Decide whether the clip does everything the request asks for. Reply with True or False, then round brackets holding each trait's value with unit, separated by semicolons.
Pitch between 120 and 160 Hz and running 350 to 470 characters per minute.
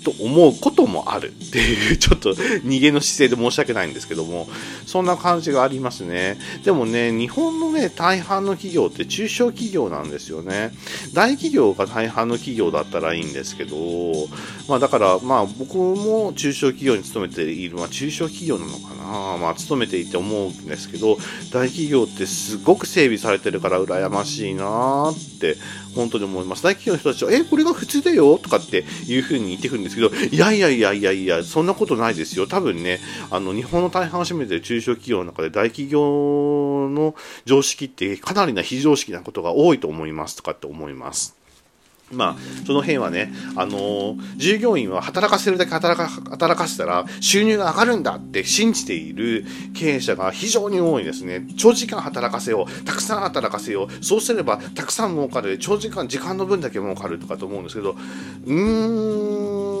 True (135 Hz; 375 characters per minute)